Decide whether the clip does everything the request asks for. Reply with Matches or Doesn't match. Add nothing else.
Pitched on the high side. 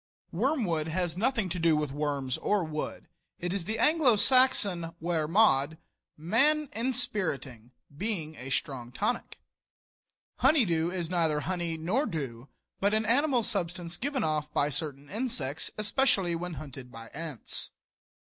Doesn't match